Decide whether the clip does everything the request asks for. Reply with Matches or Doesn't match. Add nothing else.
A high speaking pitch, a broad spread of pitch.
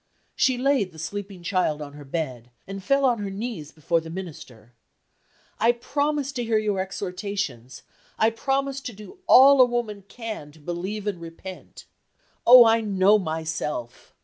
Matches